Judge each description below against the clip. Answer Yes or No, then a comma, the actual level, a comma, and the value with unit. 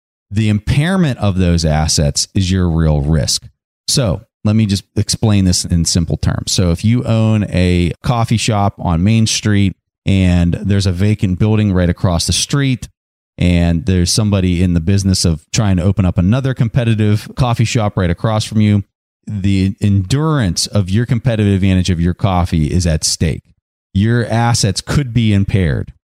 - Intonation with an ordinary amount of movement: Yes, average, 3.9 semitones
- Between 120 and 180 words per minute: Yes, average, 170 wpm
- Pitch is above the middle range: No, low, 100 Hz